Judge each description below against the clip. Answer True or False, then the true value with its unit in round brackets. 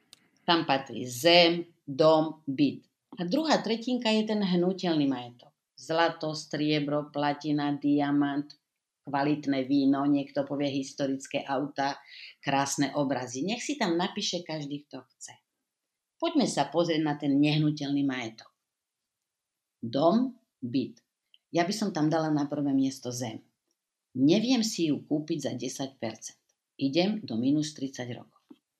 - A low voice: False (150 Hz)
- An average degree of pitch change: True (3.7 semitones)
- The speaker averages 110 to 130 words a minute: True (125 wpm)